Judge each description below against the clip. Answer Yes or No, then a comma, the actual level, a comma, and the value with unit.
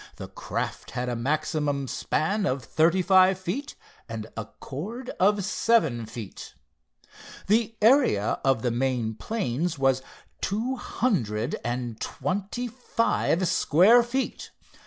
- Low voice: No, medium, 165 Hz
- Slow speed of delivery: Yes, slow, 120 wpm